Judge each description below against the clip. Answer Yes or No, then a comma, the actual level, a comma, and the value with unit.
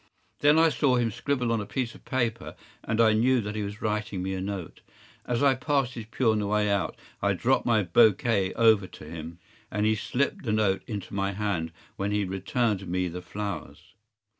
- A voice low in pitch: Yes, low, 105 Hz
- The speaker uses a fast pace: Yes, fast, 210 wpm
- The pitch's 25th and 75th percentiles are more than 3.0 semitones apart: Yes, average, 3.5 semitones